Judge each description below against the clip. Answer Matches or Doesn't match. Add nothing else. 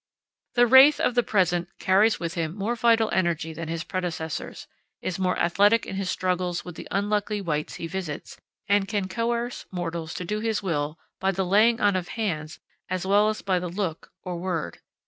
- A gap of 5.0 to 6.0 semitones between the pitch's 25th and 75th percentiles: Doesn't match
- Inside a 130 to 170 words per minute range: Doesn't match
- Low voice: Doesn't match